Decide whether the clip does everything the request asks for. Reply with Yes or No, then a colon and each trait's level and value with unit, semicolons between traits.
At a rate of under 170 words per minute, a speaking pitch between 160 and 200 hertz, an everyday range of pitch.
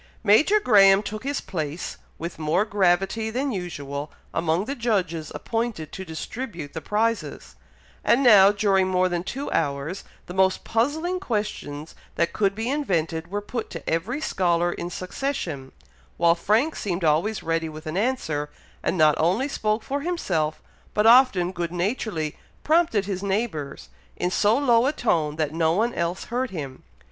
No: average, 160 wpm; high, 190 Hz; wide, 5.8 semitones